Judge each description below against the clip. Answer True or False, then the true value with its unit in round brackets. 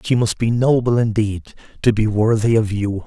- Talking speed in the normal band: True (195 wpm)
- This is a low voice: True (110 Hz)